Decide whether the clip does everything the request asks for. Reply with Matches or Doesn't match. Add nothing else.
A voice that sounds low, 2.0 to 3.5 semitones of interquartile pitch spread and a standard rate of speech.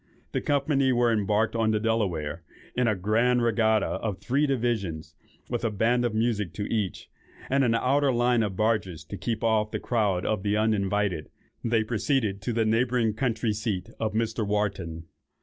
Matches